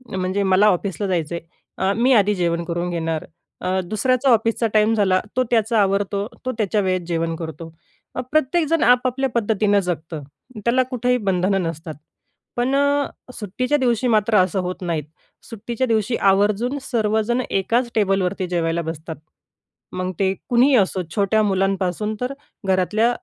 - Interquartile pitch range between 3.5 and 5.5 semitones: Yes, average, 4.4 semitones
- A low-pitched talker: No, high, 200 Hz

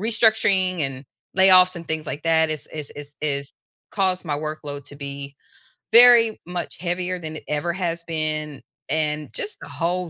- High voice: No, medium, 160 Hz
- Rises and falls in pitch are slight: No, average, 3.5 semitones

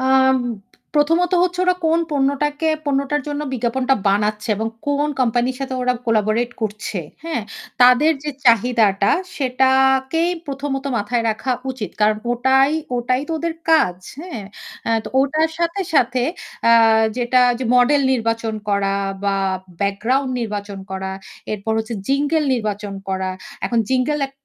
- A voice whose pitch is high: Yes, very high, 255 Hz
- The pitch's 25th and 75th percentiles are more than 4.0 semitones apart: Yes, average, 4.5 semitones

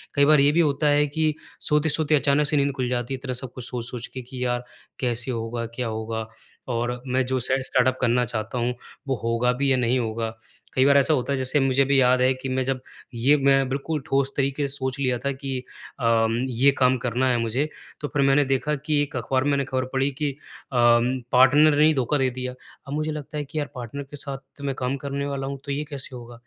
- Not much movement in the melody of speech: Yes, narrow, 2.2 semitones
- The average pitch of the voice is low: Yes, low, 130 Hz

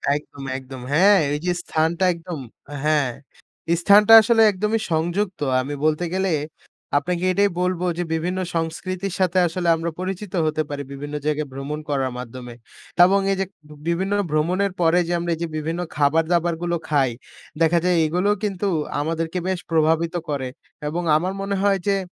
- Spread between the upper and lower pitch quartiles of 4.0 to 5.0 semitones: No, average, 3.4 semitones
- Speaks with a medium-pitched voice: Yes, medium, 170 Hz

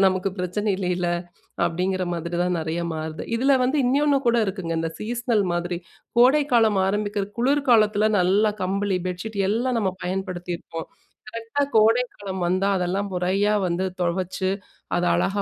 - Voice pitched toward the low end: No, high, 195 Hz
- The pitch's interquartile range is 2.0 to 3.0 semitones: No, average, 3.7 semitones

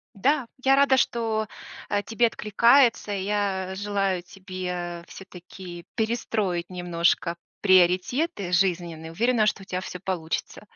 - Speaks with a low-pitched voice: No, high, 190 Hz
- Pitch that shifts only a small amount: No, average, 3.6 semitones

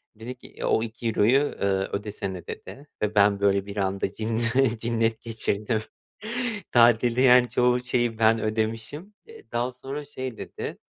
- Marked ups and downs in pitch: No, narrow, 2.5 semitones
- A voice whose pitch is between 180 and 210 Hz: No, low, 115 Hz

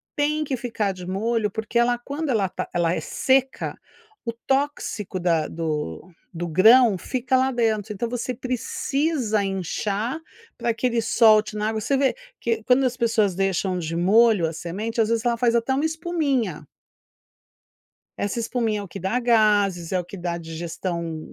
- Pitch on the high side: Yes, high, 220 Hz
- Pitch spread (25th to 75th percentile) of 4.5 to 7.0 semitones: Yes, average, 4.9 semitones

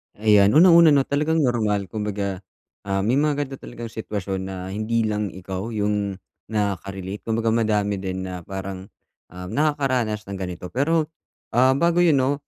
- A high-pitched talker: No, low, 105 Hz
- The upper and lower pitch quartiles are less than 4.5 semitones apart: No, wide, 5.5 semitones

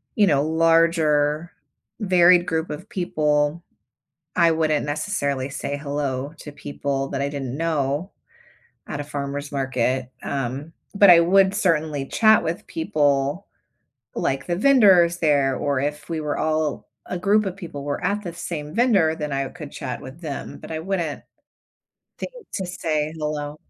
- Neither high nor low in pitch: Yes, medium, 155 Hz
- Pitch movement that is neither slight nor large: Yes, average, 3.3 semitones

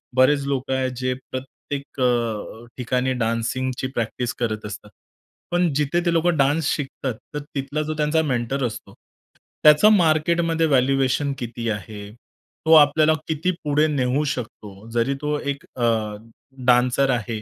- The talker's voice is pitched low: Yes, low, 130 Hz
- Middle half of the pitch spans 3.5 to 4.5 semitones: Yes, average, 4.0 semitones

